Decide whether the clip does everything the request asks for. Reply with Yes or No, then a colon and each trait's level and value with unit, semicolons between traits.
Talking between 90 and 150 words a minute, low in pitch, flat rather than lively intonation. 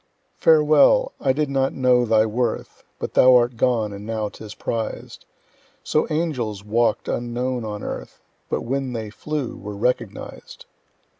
No: average, 145 wpm; low, 120 Hz; average, 3.7 semitones